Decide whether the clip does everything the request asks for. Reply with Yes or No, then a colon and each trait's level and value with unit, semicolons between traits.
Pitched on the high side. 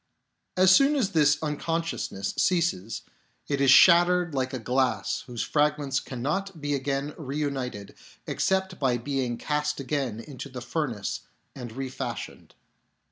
No: medium, 140 Hz